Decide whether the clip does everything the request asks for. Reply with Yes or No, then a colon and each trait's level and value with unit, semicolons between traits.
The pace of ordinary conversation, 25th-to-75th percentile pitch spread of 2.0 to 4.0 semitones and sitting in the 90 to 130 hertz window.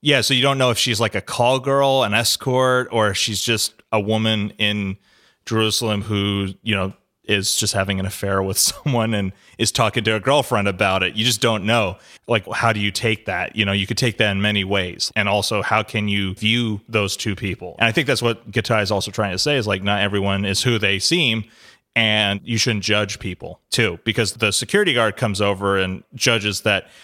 No: fast, 225 wpm; narrow, 2.6 semitones; low, 110 Hz